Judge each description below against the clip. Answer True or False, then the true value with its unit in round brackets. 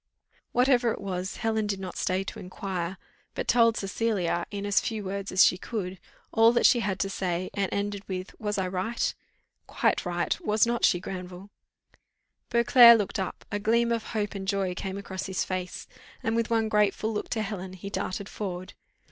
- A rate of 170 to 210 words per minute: True (190 wpm)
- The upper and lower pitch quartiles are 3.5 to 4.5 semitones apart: False (3.0 semitones)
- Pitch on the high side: True (200 Hz)